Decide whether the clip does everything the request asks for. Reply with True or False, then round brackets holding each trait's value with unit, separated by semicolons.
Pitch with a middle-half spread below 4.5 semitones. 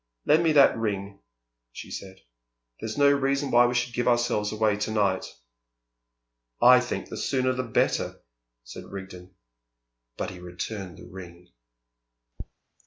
False (4.8 semitones)